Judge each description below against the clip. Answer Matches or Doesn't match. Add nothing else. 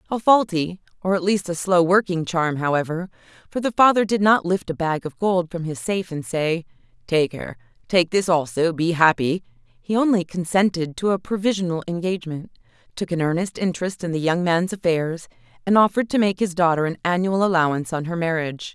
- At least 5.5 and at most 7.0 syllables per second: Matches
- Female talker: Matches